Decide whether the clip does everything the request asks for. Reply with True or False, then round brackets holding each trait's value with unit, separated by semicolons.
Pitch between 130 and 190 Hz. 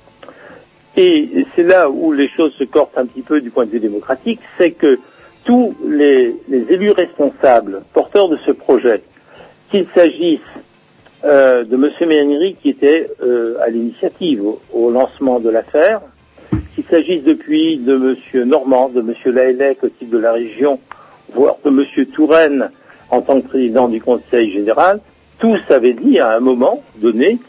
True (140 Hz)